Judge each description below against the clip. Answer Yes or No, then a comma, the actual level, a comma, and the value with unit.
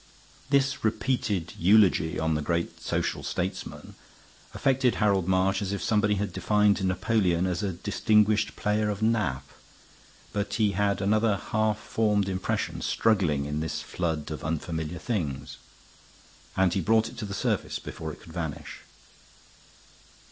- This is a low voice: Yes, low, 100 Hz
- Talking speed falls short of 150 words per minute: Yes, average, 140 wpm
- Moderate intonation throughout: Yes, average, 4.0 semitones